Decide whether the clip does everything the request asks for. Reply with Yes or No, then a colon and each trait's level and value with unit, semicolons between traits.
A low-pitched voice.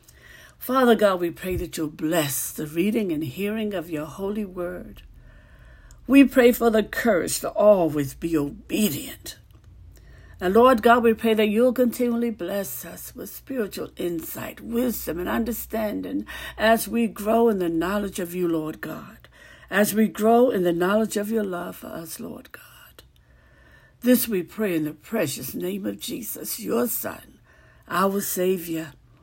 No: high, 205 Hz